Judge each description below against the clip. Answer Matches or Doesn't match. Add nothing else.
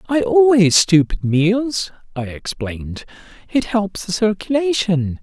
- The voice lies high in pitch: Matches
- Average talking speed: Doesn't match